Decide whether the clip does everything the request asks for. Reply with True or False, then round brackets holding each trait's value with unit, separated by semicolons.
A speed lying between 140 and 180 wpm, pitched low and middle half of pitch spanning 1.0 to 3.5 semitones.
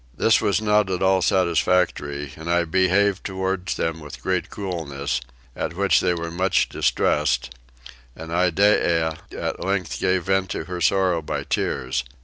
True (150 wpm; 90 Hz; 2.9 semitones)